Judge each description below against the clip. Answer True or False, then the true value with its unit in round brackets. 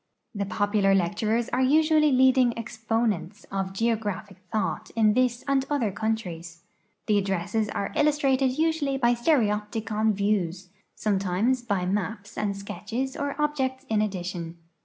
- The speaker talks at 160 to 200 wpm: False (135 wpm)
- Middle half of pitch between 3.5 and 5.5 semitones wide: True (4.7 semitones)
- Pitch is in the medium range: False (220 Hz)